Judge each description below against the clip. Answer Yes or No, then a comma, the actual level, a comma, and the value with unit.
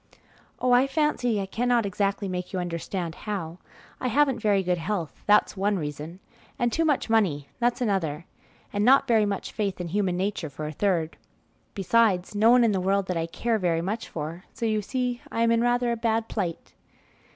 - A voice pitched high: Yes, high, 205 Hz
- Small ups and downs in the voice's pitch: No, average, 4.6 semitones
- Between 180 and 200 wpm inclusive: Yes, average, 195 wpm